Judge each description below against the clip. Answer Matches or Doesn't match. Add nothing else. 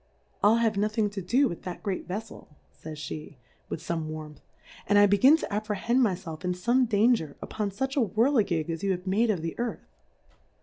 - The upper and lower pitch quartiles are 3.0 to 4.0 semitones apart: Doesn't match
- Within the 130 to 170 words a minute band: Doesn't match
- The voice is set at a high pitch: Matches